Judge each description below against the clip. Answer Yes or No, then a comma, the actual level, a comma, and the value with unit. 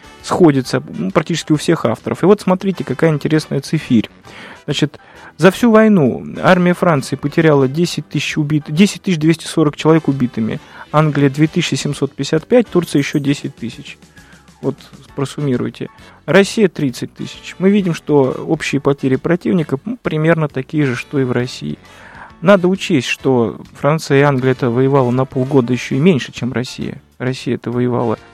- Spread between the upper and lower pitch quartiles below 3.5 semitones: No, average, 4.7 semitones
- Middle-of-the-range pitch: Yes, medium, 150 Hz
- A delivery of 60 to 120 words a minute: No, average, 145 wpm